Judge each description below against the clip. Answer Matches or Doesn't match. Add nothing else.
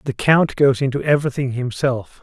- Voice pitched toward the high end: Doesn't match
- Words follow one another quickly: Doesn't match